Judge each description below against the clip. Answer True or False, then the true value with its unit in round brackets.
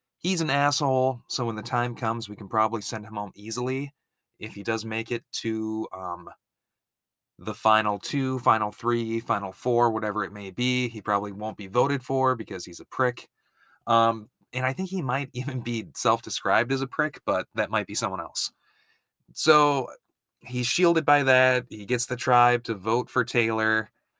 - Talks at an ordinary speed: True (185 wpm)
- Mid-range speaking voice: False (120 Hz)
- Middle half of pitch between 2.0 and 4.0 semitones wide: True (2.9 semitones)